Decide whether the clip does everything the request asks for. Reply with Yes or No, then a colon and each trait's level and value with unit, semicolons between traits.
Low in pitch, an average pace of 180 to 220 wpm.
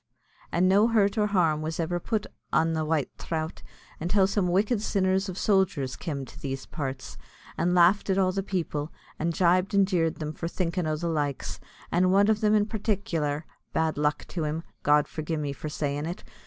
No: medium, 170 Hz; average, 195 wpm